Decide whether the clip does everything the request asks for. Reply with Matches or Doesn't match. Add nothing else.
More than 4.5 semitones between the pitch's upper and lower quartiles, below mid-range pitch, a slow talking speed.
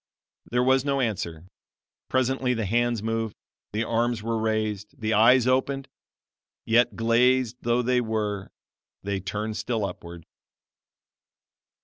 Doesn't match